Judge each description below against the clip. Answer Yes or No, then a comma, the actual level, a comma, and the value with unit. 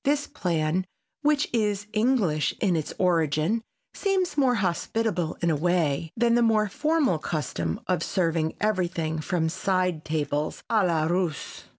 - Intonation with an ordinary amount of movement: No, wide, 5.8 semitones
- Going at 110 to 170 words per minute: Yes, average, 145 wpm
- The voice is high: No, medium, 180 Hz